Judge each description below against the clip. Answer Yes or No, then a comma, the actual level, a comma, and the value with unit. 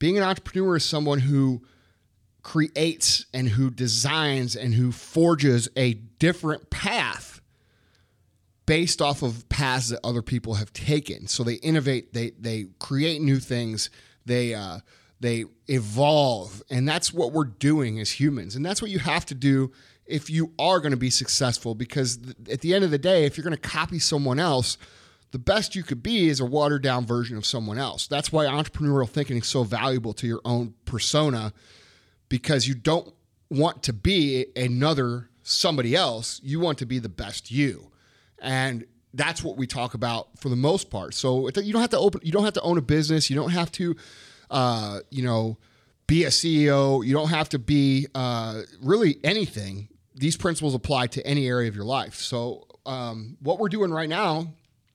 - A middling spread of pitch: Yes, average, 4.4 semitones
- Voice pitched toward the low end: Yes, low, 130 Hz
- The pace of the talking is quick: No, average, 185 wpm